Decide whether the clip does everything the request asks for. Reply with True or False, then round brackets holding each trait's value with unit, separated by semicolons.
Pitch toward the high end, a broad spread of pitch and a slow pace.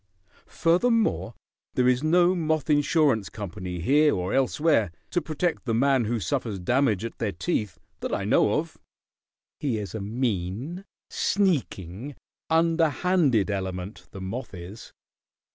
False (125 Hz; 8.0 semitones; 130 wpm)